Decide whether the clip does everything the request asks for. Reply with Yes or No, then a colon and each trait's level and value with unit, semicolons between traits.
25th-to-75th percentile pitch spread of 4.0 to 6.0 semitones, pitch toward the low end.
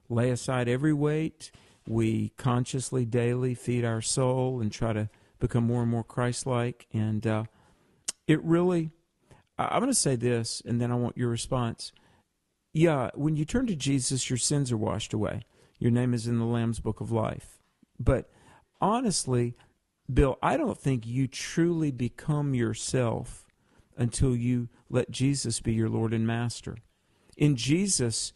No: average, 3.1 semitones; low, 120 Hz